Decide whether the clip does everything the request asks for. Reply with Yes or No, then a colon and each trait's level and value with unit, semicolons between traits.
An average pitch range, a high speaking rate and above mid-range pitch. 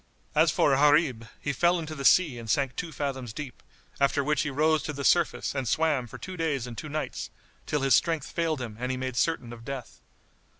No: average, 3.5 semitones; fast, 220 wpm; medium, 140 Hz